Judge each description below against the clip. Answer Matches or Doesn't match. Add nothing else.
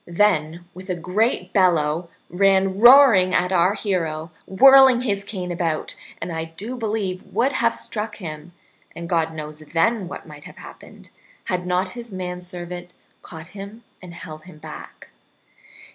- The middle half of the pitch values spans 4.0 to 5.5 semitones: Doesn't match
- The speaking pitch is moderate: Matches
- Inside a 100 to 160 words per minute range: Matches